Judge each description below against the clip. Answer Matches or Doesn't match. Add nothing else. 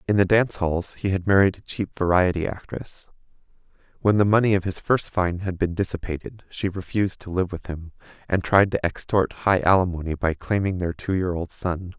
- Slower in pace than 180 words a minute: Doesn't match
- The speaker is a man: Matches